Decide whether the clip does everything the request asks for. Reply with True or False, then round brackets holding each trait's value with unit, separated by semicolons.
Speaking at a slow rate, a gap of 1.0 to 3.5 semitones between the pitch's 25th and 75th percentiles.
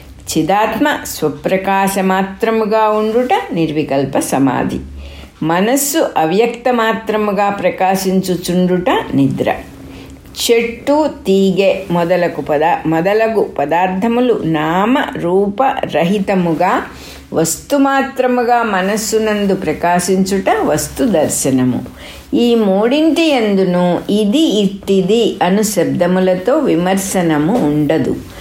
False (65 wpm; 4.9 semitones)